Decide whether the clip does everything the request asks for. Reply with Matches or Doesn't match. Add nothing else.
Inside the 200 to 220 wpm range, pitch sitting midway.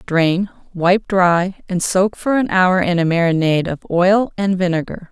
Doesn't match